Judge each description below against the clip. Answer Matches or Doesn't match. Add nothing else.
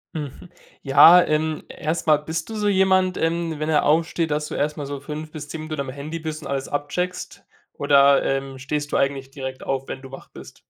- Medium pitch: Matches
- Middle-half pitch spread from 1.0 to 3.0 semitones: Matches